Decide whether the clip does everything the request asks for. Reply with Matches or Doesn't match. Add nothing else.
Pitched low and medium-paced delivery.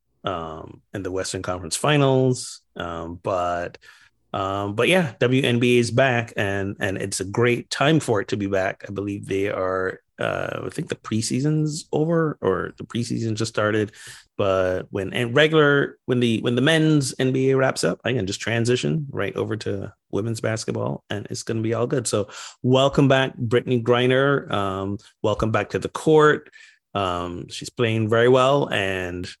Matches